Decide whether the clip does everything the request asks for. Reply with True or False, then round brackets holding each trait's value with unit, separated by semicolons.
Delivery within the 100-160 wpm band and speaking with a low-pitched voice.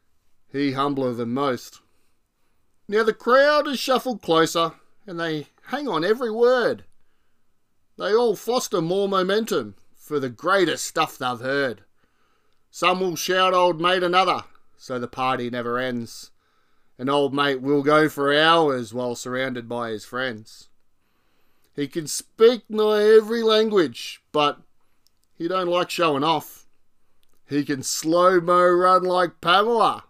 False (135 wpm; 145 Hz)